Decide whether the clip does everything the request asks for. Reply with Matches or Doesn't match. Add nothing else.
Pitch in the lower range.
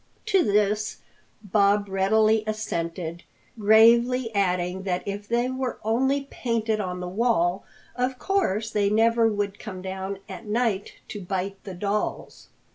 Doesn't match